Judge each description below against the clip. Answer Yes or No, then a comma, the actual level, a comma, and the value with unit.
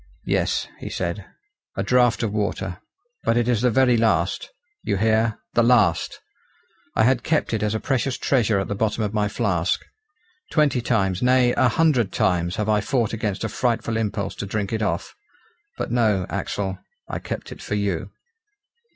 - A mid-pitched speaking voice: No, low, 110 Hz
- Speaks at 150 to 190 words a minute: Yes, average, 175 wpm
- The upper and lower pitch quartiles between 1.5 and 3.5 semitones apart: Yes, average, 3.2 semitones